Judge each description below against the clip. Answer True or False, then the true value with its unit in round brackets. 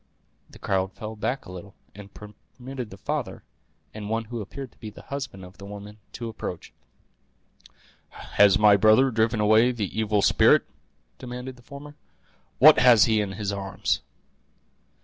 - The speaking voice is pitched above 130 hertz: False (110 Hz)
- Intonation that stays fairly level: False (3.4 semitones)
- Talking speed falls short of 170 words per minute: True (160 wpm)